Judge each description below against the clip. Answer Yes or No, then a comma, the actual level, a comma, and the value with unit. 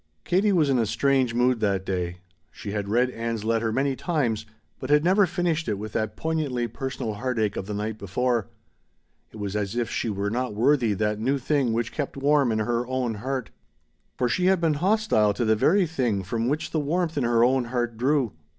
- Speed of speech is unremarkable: No, fast, 210 wpm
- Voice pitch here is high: No, low, 120 Hz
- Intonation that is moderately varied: Yes, average, 4.6 semitones